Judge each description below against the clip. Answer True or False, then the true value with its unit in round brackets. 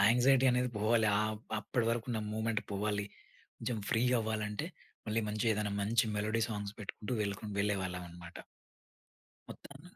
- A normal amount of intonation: False (1.9 semitones)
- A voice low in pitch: True (110 Hz)